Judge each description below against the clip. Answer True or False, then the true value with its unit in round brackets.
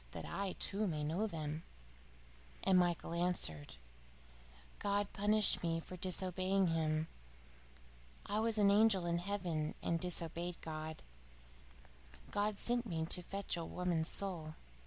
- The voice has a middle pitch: True (180 Hz)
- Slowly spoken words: True (130 wpm)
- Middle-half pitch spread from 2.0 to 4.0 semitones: True (3.5 semitones)